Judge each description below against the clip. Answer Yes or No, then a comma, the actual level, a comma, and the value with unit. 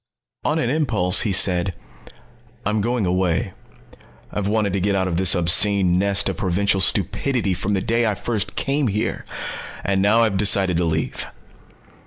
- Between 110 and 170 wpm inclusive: Yes, average, 165 wpm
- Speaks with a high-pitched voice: No, low, 100 Hz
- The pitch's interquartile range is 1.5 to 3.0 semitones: Yes, average, 2.7 semitones